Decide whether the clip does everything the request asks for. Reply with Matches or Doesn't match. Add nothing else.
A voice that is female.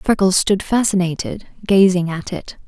Matches